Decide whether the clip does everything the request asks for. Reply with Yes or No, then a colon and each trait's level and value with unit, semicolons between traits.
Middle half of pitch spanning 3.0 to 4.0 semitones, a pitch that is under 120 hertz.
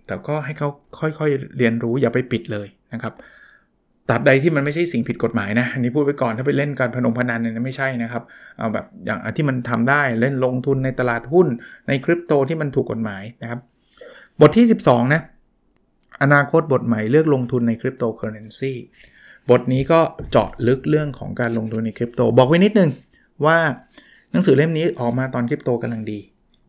No: average, 3.6 semitones; low, 130 Hz